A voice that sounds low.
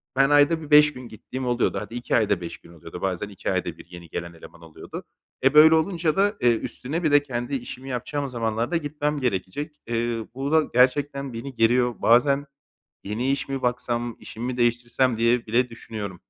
Yes: low, 125 Hz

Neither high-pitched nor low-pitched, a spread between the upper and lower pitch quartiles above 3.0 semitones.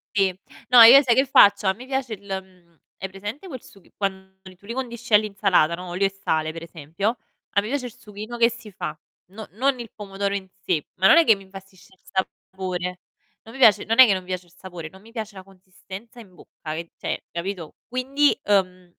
No: high, 195 Hz; average, 3.7 semitones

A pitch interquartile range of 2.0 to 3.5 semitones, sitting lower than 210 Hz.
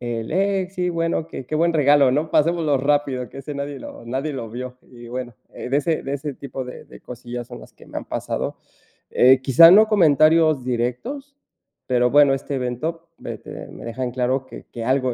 No: average, 4.1 semitones; low, 135 Hz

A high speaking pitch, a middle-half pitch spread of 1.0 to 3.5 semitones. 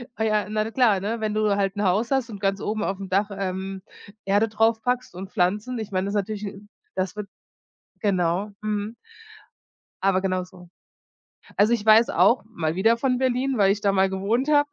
Yes: high, 205 Hz; narrow, 2.5 semitones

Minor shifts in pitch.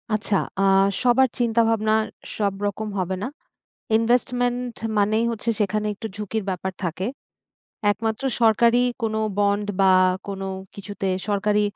Yes: narrow, 2.2 semitones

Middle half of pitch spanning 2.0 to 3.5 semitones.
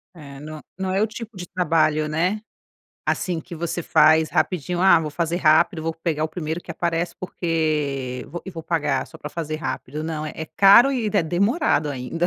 Yes: narrow, 2.6 semitones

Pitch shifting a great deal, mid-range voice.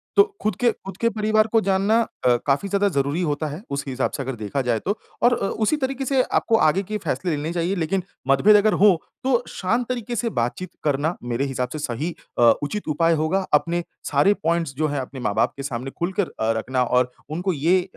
Yes: wide, 6.8 semitones; medium, 170 Hz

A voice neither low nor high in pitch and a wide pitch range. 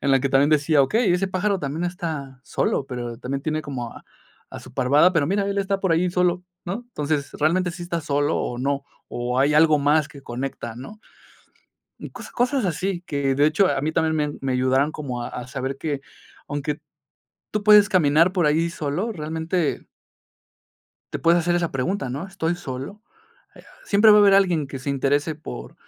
No: medium, 155 Hz; average, 4.6 semitones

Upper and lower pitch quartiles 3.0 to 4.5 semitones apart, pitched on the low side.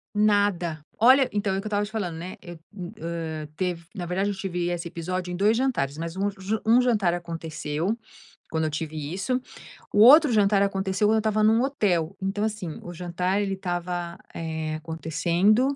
No: average, 3.7 semitones; medium, 185 Hz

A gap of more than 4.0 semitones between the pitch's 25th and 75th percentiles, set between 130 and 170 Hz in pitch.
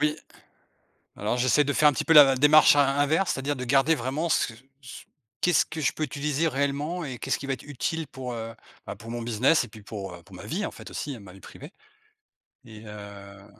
Yes: average, 4.5 semitones; low, 135 Hz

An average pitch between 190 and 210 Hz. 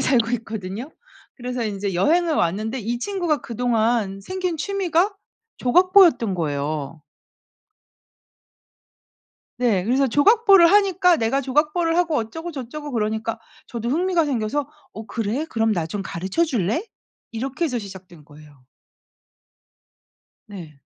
No: high, 240 Hz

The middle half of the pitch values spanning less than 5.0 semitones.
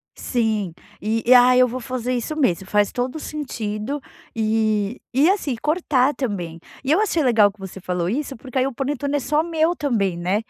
No: average, 5.3 semitones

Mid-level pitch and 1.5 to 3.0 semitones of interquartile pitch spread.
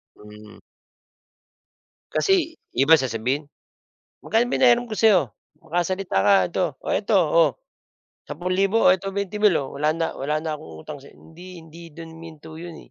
No: medium, 165 Hz; average, 5.0 semitones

